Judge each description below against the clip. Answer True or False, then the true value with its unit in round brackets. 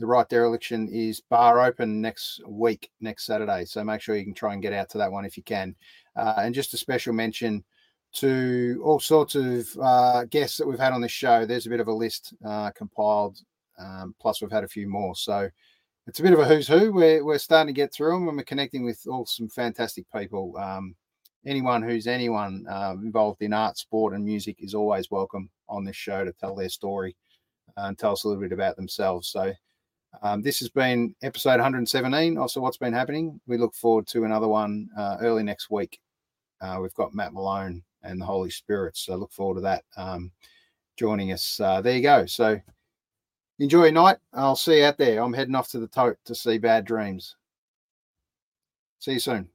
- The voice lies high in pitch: False (115 Hz)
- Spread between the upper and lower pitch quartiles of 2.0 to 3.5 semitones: False (4.1 semitones)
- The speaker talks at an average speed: False (210 wpm)